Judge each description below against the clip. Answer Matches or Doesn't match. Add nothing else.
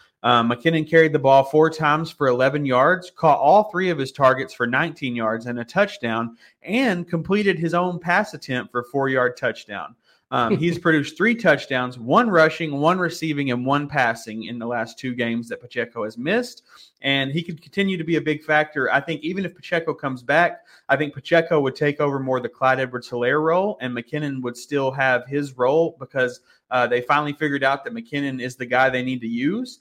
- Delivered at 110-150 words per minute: Doesn't match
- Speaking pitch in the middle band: Matches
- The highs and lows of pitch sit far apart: Doesn't match